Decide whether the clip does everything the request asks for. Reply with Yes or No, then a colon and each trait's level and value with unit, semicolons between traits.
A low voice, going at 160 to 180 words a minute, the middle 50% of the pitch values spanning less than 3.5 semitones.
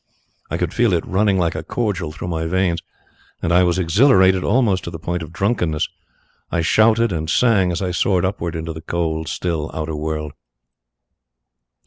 Yes: very low, 85 Hz; average, 175 wpm; average, 2.9 semitones